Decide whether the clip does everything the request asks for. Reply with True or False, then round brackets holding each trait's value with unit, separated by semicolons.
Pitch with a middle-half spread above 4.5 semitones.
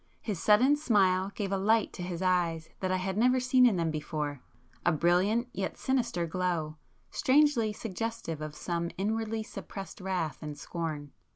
True (5.0 semitones)